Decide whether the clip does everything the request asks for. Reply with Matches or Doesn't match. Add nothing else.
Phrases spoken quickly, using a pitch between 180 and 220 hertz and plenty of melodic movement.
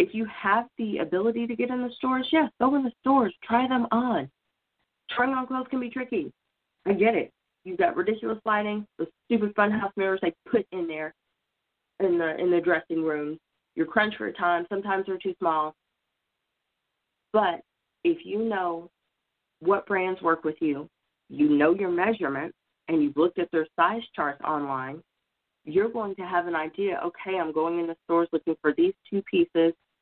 Doesn't match